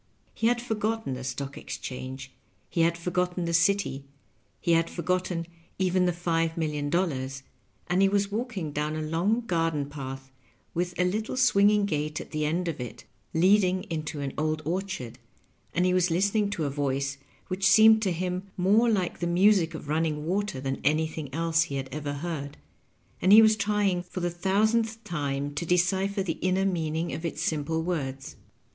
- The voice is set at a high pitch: No, medium, 170 Hz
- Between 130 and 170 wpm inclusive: No, average, 180 wpm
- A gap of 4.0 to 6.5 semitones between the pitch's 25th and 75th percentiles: Yes, average, 4.3 semitones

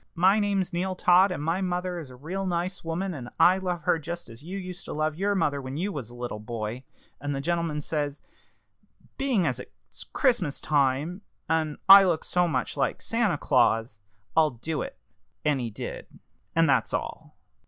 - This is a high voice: No, medium, 165 Hz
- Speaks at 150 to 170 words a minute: No, average, 195 wpm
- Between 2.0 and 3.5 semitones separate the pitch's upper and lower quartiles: No, average, 4.8 semitones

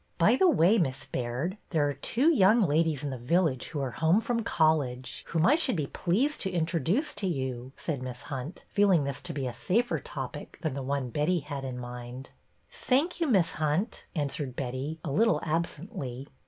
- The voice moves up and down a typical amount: No, wide, 6.1 semitones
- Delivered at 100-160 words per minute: No, average, 200 wpm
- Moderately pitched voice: Yes, medium, 155 Hz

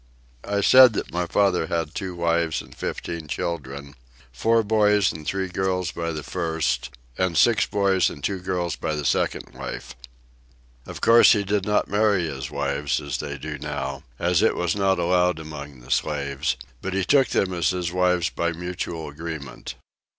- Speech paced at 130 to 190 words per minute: Yes, average, 175 wpm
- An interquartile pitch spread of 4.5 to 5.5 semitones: No, average, 4.0 semitones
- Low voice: Yes, very low, 85 Hz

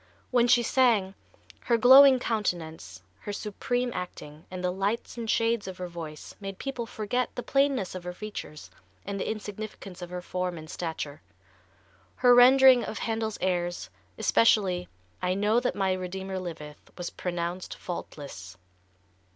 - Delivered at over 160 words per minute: No, average, 150 wpm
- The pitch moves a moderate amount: Yes, average, 4.8 semitones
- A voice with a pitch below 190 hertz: No, high, 195 Hz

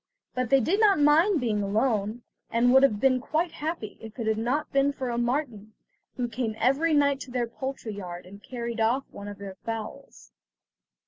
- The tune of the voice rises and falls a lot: No, average, 4.1 semitones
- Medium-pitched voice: No, high, 245 Hz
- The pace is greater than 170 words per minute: Yes, average, 195 wpm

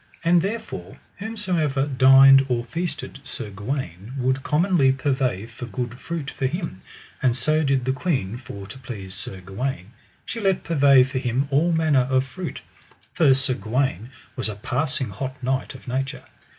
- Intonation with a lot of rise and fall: No, average, 3.4 semitones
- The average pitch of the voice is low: Yes, low, 130 Hz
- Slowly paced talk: No, average, 165 wpm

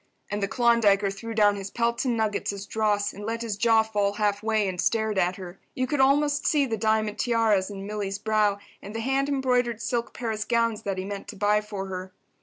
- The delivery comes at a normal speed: No, fast, 220 wpm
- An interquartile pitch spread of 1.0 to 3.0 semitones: Yes, narrow, 2.6 semitones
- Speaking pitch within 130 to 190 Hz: No, high, 215 Hz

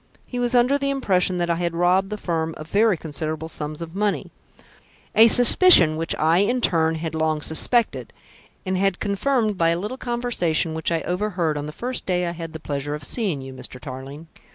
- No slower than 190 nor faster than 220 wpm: Yes, average, 200 wpm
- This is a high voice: No, medium, 175 Hz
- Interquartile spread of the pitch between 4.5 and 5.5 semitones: Yes, average, 5.0 semitones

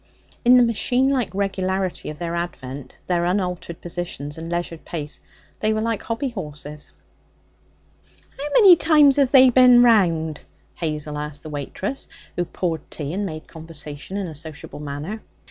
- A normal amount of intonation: No, wide, 6.9 semitones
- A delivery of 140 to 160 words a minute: Yes, average, 155 wpm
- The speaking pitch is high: No, medium, 175 Hz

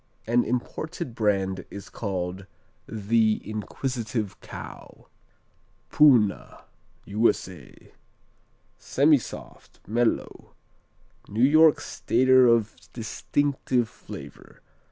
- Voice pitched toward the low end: Yes, low, 115 Hz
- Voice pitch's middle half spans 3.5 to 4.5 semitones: Yes, average, 3.9 semitones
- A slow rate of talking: Yes, slow, 70 wpm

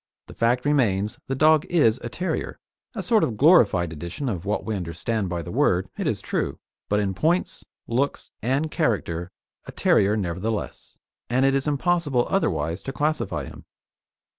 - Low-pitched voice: Yes, low, 115 Hz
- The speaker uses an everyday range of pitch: No, wide, 7.3 semitones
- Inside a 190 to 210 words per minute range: No, average, 165 wpm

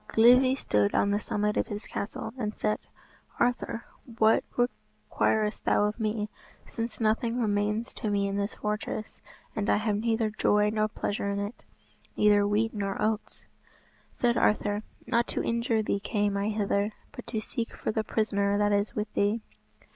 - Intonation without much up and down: Yes, narrow, 1.6 semitones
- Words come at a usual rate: Yes, average, 170 wpm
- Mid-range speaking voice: No, high, 215 Hz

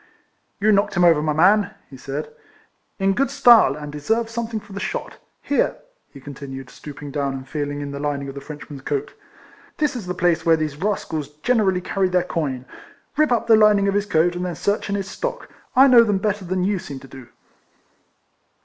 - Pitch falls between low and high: Yes, medium, 180 Hz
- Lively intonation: Yes, wide, 6.3 semitones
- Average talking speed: No, fast, 210 wpm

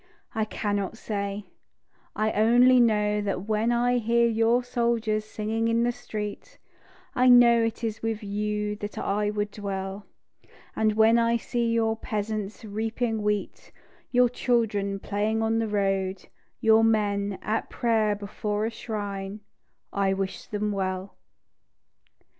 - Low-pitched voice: No, high, 215 Hz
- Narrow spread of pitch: Yes, narrow, 1.9 semitones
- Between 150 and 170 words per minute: No, slow, 135 wpm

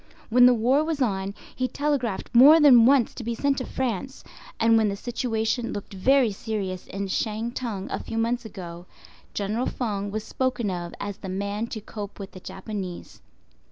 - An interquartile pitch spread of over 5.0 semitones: No, average, 3.9 semitones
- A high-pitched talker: Yes, high, 225 Hz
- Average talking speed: Yes, average, 180 wpm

